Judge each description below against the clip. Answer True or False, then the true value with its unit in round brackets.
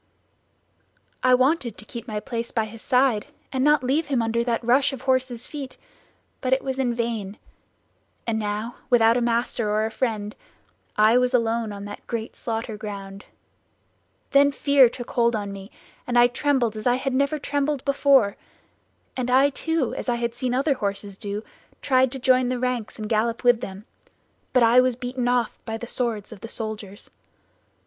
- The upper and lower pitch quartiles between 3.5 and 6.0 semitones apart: False (2.9 semitones)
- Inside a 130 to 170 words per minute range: False (185 wpm)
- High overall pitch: True (240 Hz)